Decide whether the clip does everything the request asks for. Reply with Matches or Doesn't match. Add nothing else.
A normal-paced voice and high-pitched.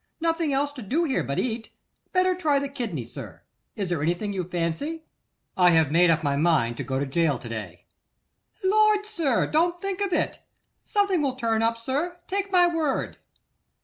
Matches